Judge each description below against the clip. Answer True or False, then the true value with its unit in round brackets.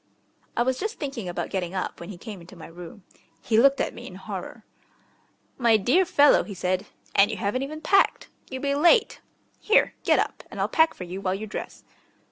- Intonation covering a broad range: True (7.1 semitones)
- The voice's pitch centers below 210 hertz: False (220 Hz)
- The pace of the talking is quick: True (210 wpm)